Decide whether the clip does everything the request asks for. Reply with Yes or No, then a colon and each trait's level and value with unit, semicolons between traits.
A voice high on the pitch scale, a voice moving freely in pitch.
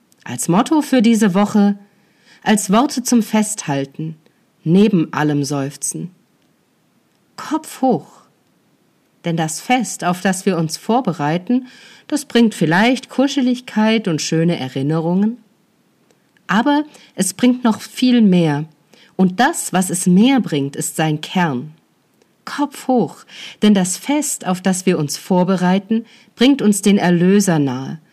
Yes: high, 200 Hz; wide, 5.9 semitones